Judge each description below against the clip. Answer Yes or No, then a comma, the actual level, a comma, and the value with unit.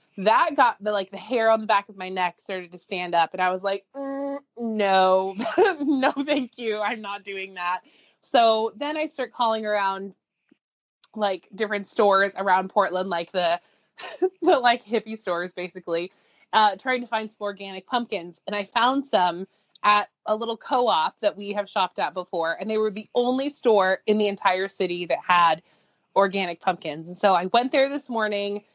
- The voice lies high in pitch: Yes, high, 205 Hz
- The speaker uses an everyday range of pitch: Yes, average, 3.7 semitones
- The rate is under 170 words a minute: No, average, 185 wpm